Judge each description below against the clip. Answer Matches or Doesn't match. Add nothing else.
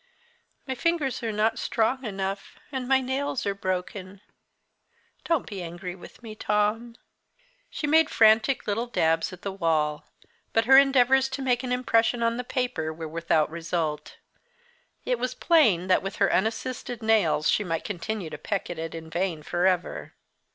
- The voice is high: Matches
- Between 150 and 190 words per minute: Matches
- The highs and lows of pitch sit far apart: Matches